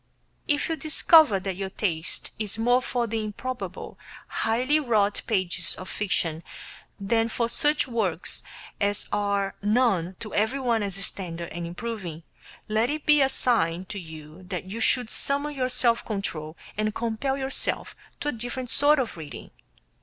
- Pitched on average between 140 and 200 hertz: No, high, 220 Hz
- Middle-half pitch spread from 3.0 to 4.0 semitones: No, average, 4.9 semitones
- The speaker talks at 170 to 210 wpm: No, average, 155 wpm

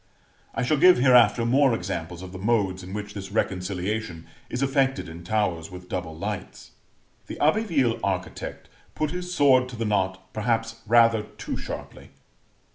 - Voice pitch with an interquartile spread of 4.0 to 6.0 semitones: Yes, average, 5.2 semitones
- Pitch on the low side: Yes, low, 110 Hz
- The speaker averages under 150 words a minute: No, average, 155 wpm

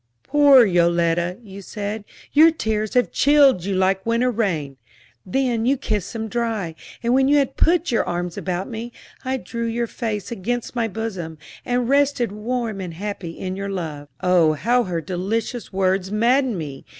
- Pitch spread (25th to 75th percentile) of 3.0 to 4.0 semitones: No, average, 5.0 semitones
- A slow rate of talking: No, average, 170 wpm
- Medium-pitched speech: No, high, 215 Hz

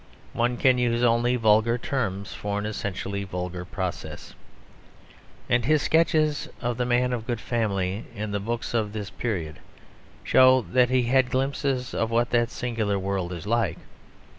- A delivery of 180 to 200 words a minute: No, average, 165 wpm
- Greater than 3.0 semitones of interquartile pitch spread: Yes, average, 3.5 semitones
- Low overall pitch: Yes, low, 115 Hz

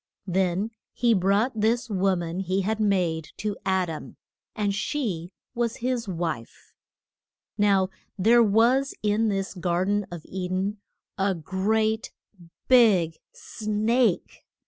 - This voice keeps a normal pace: No, slow, 125 wpm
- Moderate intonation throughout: Yes, average, 3.1 semitones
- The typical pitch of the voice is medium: No, high, 200 Hz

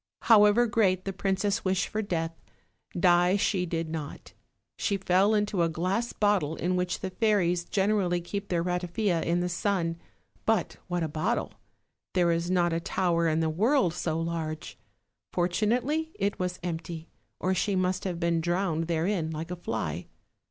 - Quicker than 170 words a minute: No, average, 165 wpm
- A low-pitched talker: No, medium, 180 Hz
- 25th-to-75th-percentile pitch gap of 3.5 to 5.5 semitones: No, average, 3.0 semitones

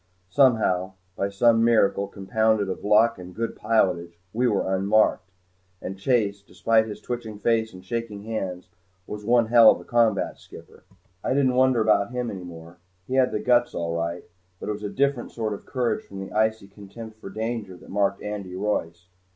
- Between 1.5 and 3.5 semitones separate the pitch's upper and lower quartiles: Yes, average, 3.1 semitones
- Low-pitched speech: Yes, low, 105 Hz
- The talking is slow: No, average, 185 wpm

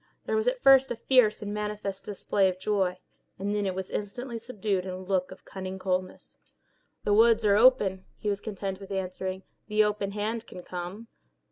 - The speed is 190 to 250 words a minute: Yes, average, 195 wpm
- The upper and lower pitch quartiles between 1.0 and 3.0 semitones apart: Yes, narrow, 2.4 semitones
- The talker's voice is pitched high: Yes, high, 200 Hz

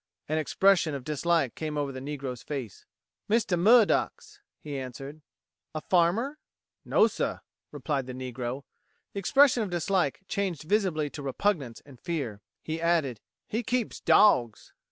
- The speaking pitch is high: No, medium, 155 Hz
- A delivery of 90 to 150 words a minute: Yes, average, 140 wpm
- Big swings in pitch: Yes, wide, 6.4 semitones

